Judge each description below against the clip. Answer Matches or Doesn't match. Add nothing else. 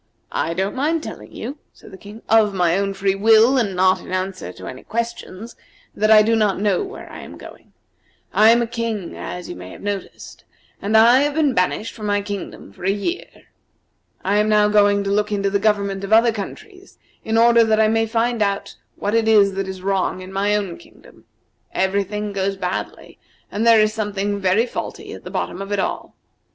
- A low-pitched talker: Doesn't match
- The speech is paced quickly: Matches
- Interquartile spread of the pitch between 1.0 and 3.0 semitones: Matches